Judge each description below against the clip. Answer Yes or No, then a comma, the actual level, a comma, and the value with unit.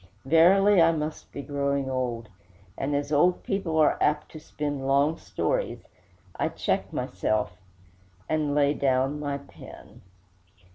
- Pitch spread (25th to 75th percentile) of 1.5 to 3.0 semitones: Yes, narrow, 2.4 semitones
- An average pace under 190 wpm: Yes, slow, 135 wpm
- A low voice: No, medium, 145 Hz